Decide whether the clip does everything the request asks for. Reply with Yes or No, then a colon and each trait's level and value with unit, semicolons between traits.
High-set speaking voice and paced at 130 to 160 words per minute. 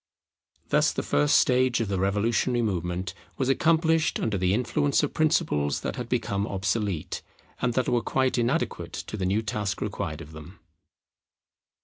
No: low, 105 Hz; average, 155 wpm